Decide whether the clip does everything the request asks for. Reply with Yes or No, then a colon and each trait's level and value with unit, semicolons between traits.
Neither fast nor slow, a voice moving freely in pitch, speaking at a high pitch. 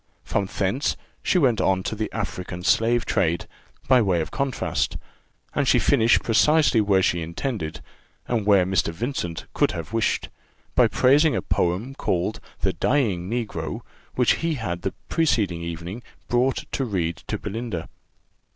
No: average, 150 wpm; wide, 5.8 semitones; low, 105 Hz